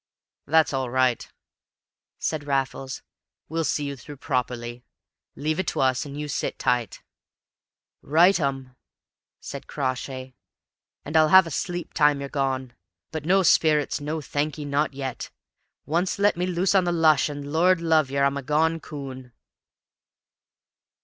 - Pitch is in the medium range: Yes, medium, 145 Hz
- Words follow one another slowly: No, average, 145 wpm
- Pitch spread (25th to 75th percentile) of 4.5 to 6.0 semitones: No, average, 3.2 semitones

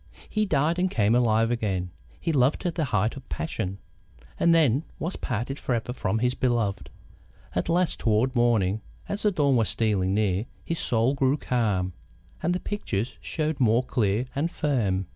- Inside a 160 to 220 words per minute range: Yes, average, 170 wpm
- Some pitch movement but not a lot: No, wide, 5.8 semitones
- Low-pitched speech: Yes, low, 120 Hz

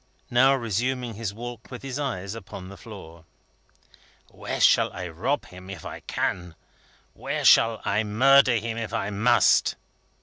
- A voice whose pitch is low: Yes, low, 110 Hz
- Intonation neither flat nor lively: Yes, average, 4.3 semitones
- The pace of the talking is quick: No, average, 155 wpm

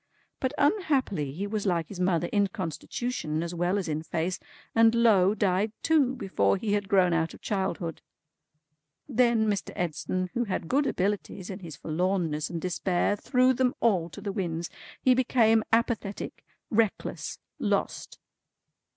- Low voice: No, high, 195 Hz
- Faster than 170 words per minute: No, average, 150 wpm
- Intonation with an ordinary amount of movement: Yes, average, 4.7 semitones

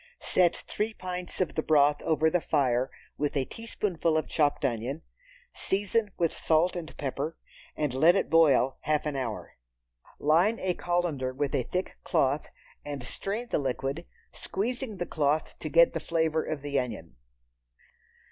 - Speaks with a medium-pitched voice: Yes, medium, 155 Hz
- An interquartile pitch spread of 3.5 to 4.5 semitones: Yes, average, 4.2 semitones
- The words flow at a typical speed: Yes, average, 155 wpm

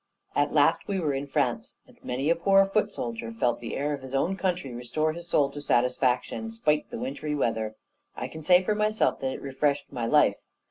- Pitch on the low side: No, medium, 145 Hz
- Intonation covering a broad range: Yes, wide, 6.4 semitones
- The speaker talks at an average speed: No, fast, 220 wpm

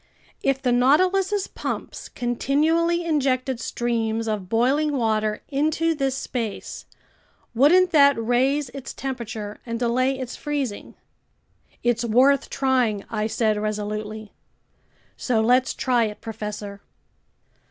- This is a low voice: No, high, 245 Hz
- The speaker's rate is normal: No, slow, 110 wpm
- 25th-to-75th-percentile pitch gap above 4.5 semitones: No, average, 4.0 semitones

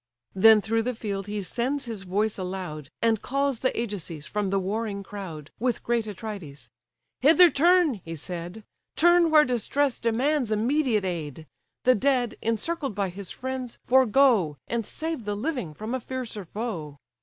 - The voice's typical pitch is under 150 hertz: No, high, 220 Hz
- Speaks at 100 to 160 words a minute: Yes, average, 155 wpm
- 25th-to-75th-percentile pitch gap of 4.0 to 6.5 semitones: Yes, average, 5.1 semitones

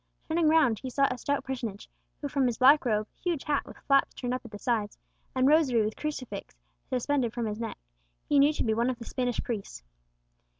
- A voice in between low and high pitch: No, very high, 255 Hz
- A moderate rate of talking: No, fast, 215 wpm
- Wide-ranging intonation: No, average, 3.8 semitones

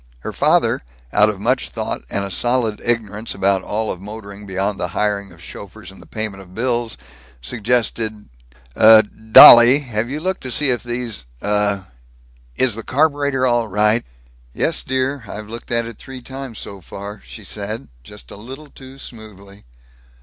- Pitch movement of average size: Yes, average, 3.5 semitones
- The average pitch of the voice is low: Yes, low, 110 Hz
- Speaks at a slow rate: No, average, 170 wpm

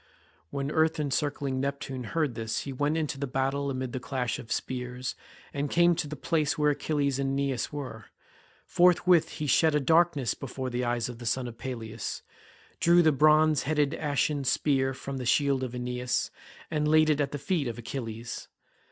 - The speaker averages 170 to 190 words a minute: Yes, average, 185 wpm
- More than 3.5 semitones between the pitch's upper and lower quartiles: No, average, 3.2 semitones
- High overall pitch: No, medium, 140 Hz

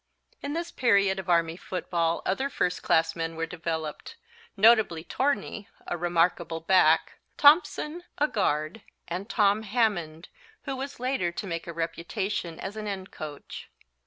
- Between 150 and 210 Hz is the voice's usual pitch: Yes, medium, 185 Hz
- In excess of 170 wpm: No, average, 145 wpm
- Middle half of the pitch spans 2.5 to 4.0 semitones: No, average, 4.9 semitones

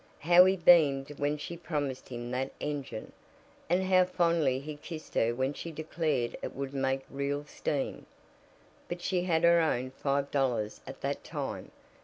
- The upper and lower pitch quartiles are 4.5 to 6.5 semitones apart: No, average, 4.1 semitones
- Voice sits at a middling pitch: Yes, medium, 145 Hz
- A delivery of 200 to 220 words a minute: No, average, 165 wpm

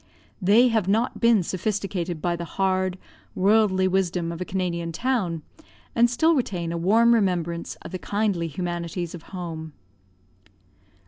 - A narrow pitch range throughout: No, average, 3.8 semitones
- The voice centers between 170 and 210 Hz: Yes, medium, 185 Hz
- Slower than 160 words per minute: Yes, average, 140 wpm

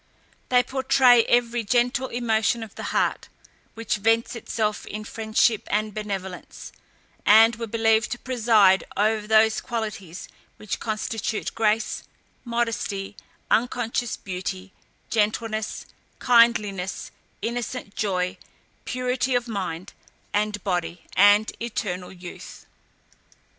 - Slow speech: Yes, slow, 105 wpm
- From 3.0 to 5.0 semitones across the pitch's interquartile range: No, narrow, 2.6 semitones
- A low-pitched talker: No, high, 220 Hz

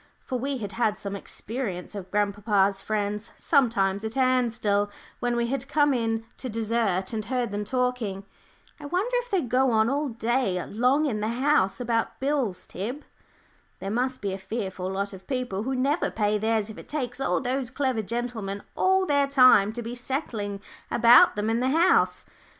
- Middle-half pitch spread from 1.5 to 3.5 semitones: No, average, 4.1 semitones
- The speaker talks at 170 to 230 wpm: Yes, average, 180 wpm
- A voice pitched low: No, high, 235 Hz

